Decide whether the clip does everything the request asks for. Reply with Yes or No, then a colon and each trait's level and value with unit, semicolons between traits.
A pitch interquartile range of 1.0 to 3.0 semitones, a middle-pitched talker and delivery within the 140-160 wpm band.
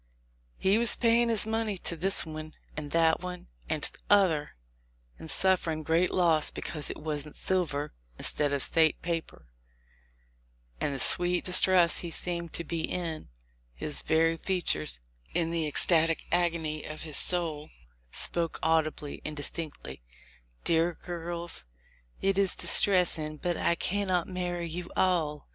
Yes: narrow, 2.6 semitones; medium, 165 Hz; average, 145 wpm